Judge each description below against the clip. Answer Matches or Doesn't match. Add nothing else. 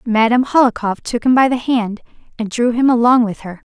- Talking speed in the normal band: Doesn't match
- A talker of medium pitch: Doesn't match